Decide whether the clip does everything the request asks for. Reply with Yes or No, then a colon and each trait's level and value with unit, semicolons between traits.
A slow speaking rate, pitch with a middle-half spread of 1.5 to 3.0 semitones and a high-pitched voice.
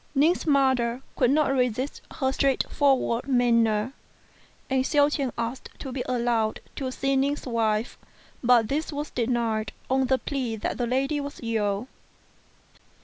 No: average, 145 wpm; average, 2.7 semitones; very high, 255 Hz